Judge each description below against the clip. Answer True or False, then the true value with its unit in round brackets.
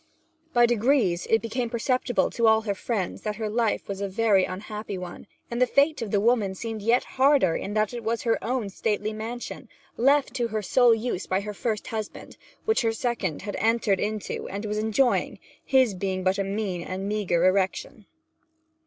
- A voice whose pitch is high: True (215 Hz)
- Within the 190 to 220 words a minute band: True (195 wpm)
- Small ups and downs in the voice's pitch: False (3.1 semitones)